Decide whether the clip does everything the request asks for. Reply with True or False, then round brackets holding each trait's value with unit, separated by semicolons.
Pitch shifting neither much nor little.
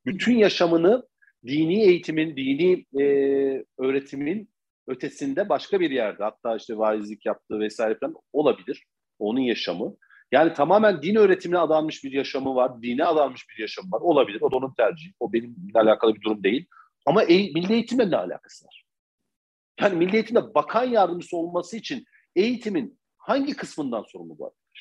False (8.6 semitones)